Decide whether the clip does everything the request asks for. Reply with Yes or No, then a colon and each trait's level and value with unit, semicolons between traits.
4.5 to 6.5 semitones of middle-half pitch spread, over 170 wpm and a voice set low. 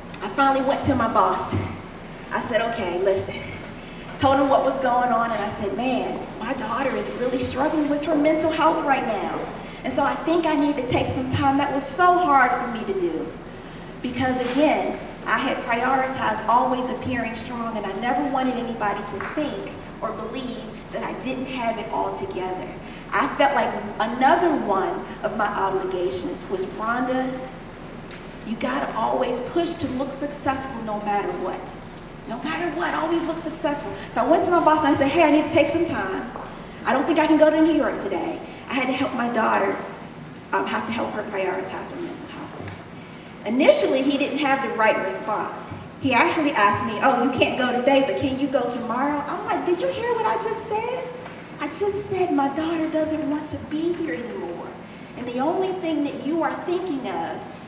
No: average, 4.9 semitones; average, 200 wpm; very high, 275 Hz